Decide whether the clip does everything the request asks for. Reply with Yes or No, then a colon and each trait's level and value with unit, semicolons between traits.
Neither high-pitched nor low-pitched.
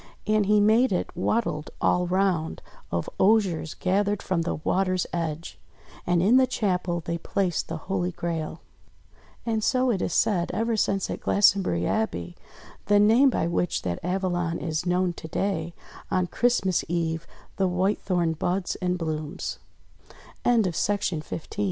Yes: medium, 180 Hz